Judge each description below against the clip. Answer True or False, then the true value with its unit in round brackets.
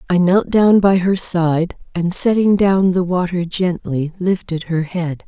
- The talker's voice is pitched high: False (180 Hz)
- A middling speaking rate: True (170 wpm)